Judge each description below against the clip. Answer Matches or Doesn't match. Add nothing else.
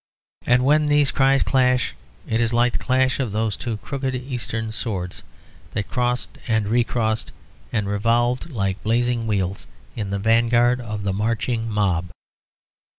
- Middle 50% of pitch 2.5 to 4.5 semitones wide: Matches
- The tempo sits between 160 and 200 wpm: Doesn't match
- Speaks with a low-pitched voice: Matches